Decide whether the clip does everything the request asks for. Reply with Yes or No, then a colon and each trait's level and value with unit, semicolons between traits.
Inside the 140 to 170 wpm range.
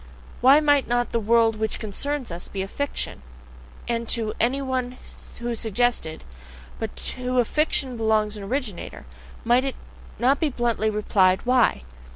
Yes: average, 155 wpm